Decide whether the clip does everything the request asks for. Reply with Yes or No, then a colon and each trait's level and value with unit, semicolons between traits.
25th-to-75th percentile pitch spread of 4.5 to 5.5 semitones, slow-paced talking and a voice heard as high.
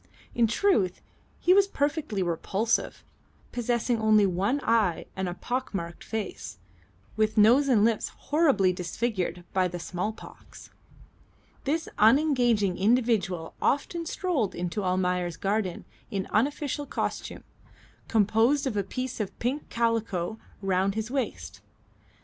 Yes: average, 5.2 semitones; slow, 120 wpm; high, 220 Hz